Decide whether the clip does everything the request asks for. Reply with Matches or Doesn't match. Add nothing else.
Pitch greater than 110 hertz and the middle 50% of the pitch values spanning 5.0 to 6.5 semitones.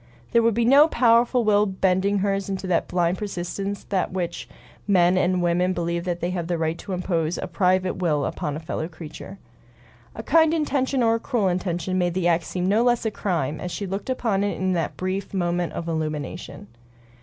Doesn't match